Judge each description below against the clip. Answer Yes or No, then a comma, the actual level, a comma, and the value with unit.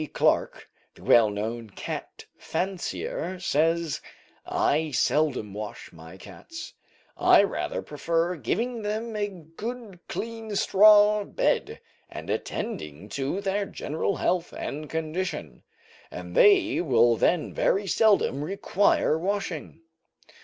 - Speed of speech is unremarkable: No, slow, 110 wpm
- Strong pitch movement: Yes, wide, 6.4 semitones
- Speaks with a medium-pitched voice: Yes, medium, 175 Hz